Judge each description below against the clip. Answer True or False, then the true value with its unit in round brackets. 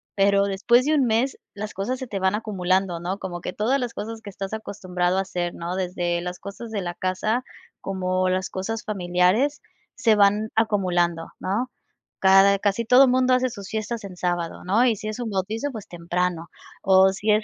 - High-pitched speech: True (200 Hz)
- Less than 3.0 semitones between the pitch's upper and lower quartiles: False (3.3 semitones)